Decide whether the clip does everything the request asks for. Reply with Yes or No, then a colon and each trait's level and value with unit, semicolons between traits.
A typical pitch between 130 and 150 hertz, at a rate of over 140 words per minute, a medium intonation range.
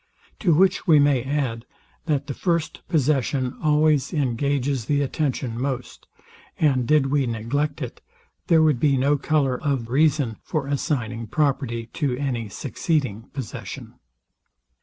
No: medium, 140 Hz; slow, 135 wpm; average, 3.3 semitones